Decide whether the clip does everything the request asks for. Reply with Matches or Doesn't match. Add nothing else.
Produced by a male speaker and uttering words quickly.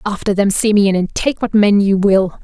Doesn't match